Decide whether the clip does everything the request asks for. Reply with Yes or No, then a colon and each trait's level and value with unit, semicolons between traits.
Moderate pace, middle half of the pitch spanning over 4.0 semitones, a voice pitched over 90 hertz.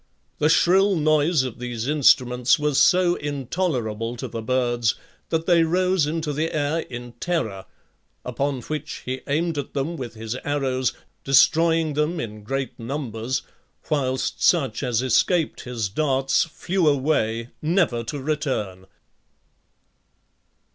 No: slow, 130 wpm; average, 4.5 semitones; medium, 140 Hz